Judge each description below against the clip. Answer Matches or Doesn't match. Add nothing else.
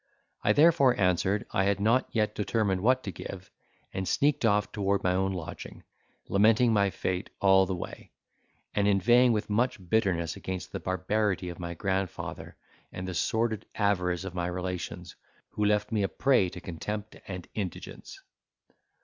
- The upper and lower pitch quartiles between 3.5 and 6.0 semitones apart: Doesn't match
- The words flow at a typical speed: Matches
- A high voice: Doesn't match